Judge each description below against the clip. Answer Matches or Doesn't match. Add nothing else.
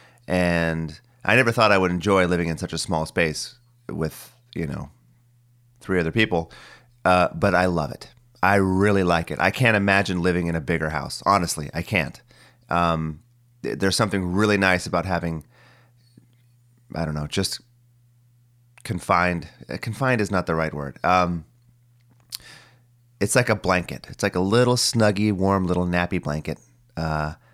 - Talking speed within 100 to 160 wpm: Matches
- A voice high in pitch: Doesn't match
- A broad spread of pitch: Matches